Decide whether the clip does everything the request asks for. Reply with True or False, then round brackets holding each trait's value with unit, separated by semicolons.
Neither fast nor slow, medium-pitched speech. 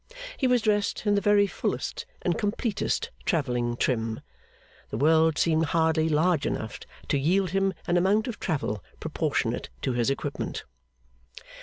True (145 wpm; 165 Hz)